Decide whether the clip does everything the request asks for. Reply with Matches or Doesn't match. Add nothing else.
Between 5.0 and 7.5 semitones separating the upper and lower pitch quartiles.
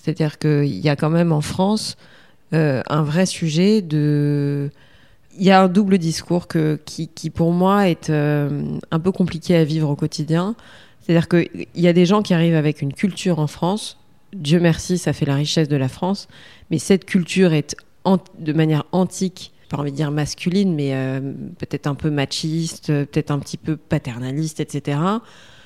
Doesn't match